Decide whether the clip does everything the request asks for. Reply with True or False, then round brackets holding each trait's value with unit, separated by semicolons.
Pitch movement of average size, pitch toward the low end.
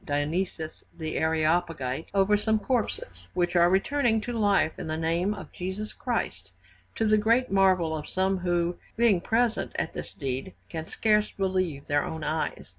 False (4.7 semitones; 180 Hz)